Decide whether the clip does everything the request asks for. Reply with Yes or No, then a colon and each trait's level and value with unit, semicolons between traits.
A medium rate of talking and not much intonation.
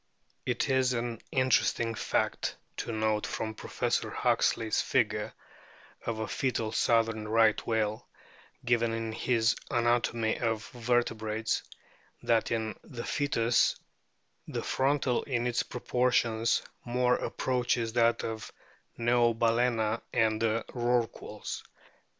No: slow, 110 wpm; narrow, 1.5 semitones